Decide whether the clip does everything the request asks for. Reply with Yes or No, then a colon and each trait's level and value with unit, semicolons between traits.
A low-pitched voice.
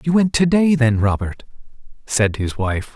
Yes: low, 130 Hz